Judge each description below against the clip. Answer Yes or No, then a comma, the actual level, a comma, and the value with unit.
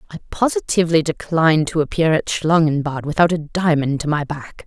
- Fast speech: No, average, 165 wpm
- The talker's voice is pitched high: No, medium, 155 Hz